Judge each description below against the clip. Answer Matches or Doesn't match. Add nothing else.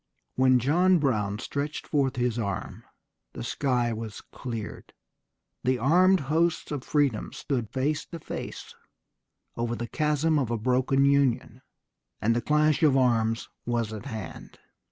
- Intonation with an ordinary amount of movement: Matches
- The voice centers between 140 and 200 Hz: Doesn't match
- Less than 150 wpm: Matches